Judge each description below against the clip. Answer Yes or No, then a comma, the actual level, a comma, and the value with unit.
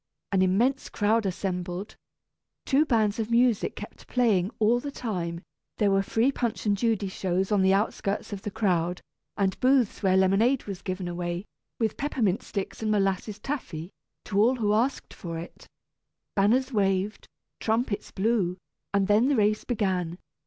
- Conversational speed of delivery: Yes, average, 160 wpm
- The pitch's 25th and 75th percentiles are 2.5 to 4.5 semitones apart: Yes, average, 3.4 semitones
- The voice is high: Yes, high, 205 Hz